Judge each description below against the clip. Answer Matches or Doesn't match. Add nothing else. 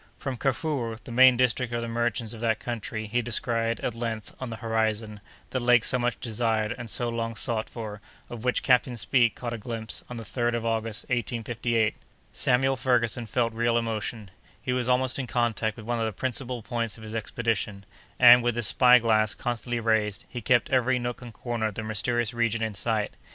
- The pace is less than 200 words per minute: Doesn't match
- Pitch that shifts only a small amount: Matches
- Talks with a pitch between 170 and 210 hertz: Doesn't match